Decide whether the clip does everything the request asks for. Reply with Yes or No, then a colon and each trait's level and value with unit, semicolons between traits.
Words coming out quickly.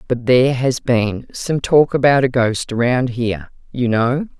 No: average, 175 wpm